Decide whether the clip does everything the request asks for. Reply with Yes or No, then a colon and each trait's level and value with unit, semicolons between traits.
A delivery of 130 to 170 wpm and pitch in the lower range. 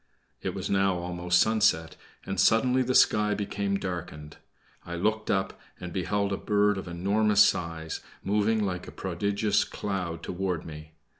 Yes: average, 150 wpm; very low, 95 Hz